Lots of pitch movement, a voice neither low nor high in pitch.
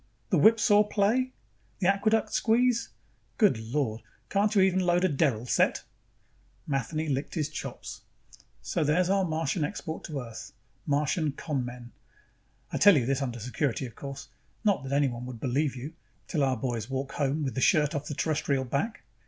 Yes: wide, 5.8 semitones; medium, 145 Hz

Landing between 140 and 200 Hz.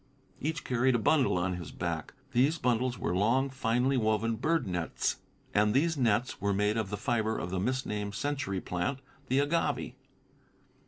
No: low, 115 Hz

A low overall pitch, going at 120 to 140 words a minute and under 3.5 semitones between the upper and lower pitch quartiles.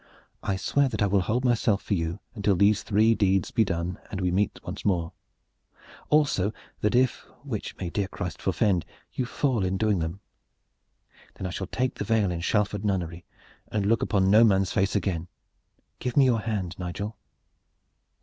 No: low, 100 Hz; average, 180 wpm; average, 3.1 semitones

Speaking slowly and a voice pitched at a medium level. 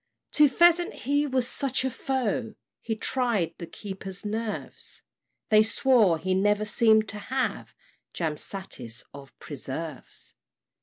No: slow, 125 wpm; high, 215 Hz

